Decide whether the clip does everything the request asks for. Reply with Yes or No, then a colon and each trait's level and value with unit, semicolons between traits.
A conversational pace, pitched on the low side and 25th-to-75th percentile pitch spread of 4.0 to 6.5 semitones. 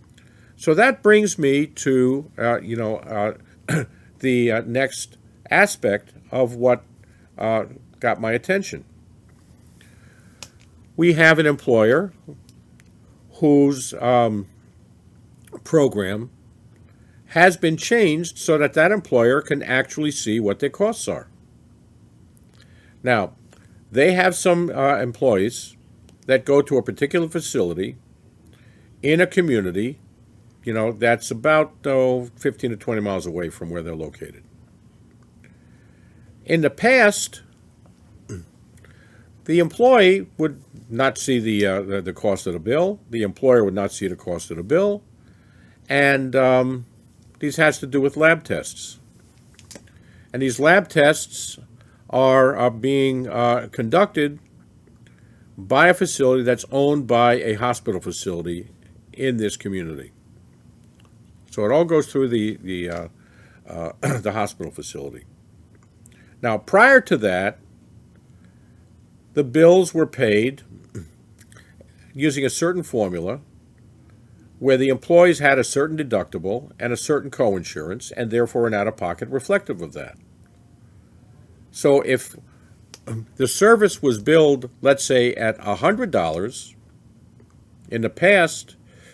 No: slow, 120 wpm; low, 120 Hz; average, 4.5 semitones